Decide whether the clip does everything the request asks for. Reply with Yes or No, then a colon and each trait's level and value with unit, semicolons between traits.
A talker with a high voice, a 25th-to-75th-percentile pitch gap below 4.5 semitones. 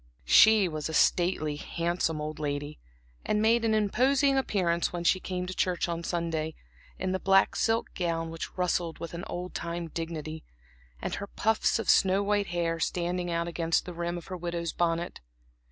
No: medium, 175 Hz; narrow, 2.4 semitones